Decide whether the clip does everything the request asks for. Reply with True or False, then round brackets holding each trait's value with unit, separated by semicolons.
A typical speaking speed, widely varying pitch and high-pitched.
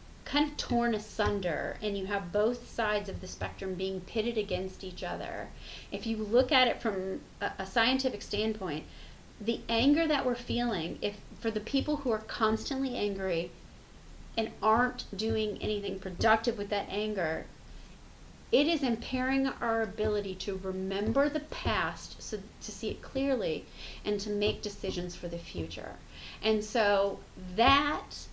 False (150 wpm; 3.2 semitones; 215 Hz)